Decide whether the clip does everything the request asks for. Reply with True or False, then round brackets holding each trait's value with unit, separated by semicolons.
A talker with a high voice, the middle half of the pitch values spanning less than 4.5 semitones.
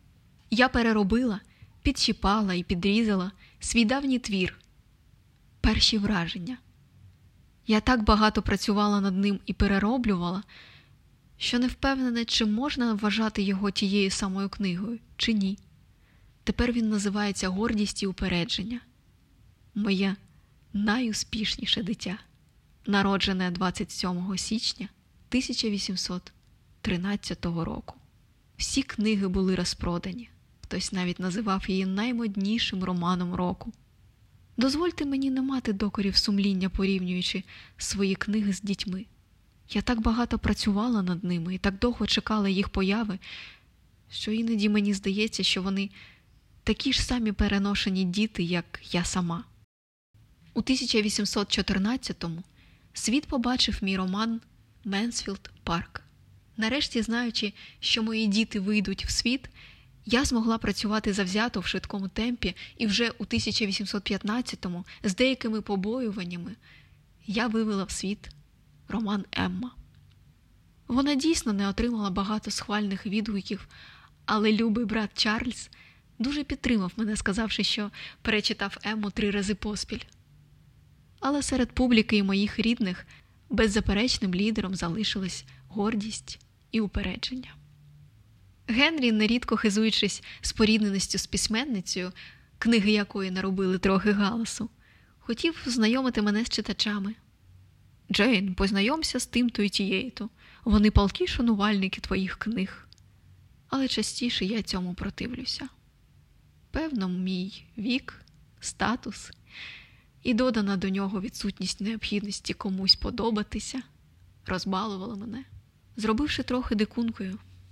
True (210 Hz; 2.9 semitones)